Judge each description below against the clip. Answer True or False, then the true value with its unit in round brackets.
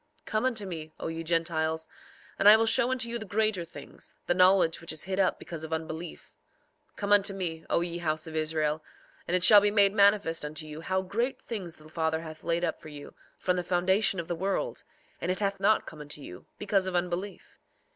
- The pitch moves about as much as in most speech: True (3.8 semitones)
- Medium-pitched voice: True (175 Hz)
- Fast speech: True (225 wpm)